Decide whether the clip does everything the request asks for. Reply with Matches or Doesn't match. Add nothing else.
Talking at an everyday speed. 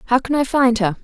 Doesn't match